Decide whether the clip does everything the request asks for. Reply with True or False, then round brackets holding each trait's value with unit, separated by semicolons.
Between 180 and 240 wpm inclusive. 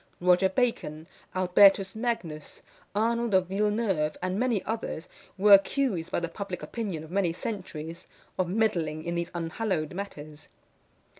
False (135 wpm)